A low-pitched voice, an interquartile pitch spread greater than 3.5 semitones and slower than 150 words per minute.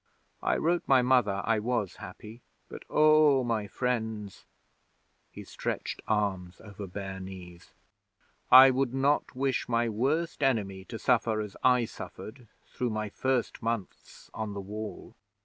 Yes: low, 115 Hz; average, 4.0 semitones; average, 140 wpm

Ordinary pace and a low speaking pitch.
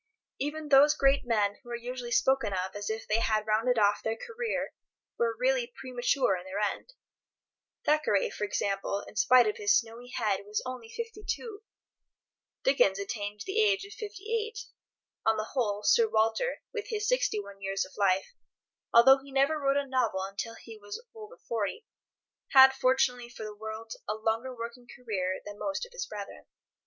No: average, 170 wpm; high, 245 Hz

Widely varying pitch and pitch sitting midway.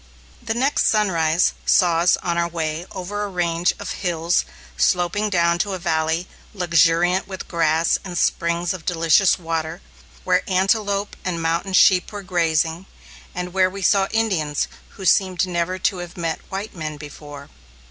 No: narrow, 2.4 semitones; medium, 175 Hz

